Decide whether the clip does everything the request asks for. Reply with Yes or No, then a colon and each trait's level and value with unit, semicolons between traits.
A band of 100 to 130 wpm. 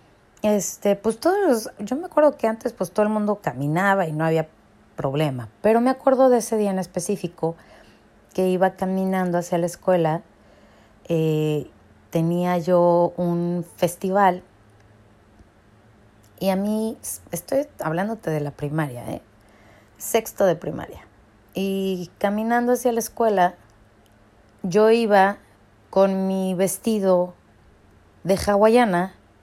Yes: slow, 125 wpm